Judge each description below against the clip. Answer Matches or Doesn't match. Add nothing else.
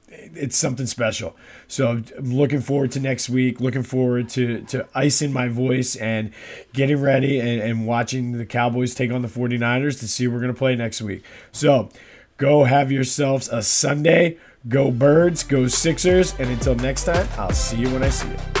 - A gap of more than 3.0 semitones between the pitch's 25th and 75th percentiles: Doesn't match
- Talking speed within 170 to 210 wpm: Matches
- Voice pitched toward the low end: Matches